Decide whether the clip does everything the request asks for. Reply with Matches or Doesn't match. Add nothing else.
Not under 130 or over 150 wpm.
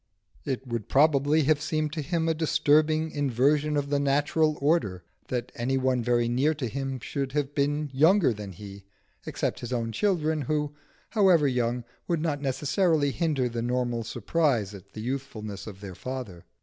Doesn't match